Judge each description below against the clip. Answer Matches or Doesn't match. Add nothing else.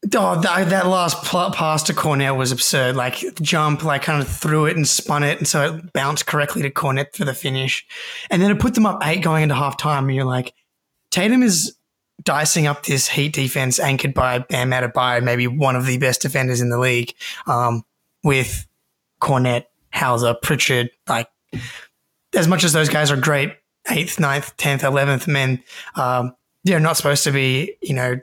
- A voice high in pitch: Doesn't match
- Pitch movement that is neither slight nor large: Matches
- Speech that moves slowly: Doesn't match